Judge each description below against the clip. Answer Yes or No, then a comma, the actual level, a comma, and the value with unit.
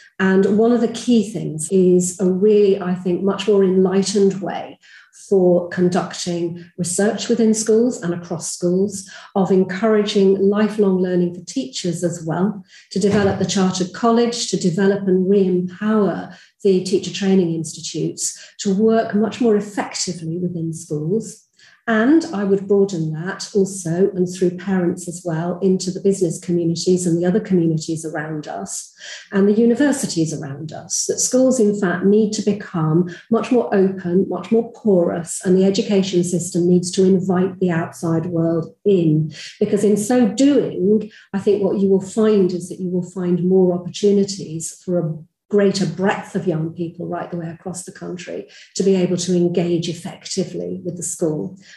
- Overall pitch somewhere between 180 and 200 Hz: Yes, high, 190 Hz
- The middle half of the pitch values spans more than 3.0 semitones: No, average, 2.7 semitones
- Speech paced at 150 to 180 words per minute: Yes, average, 165 wpm